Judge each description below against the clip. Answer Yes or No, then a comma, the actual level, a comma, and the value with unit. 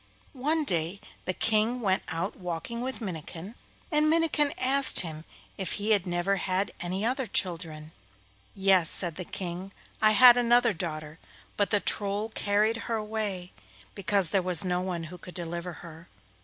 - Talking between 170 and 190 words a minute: No, average, 160 wpm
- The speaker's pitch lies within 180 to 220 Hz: Yes, high, 190 Hz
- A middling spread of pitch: Yes, average, 4.1 semitones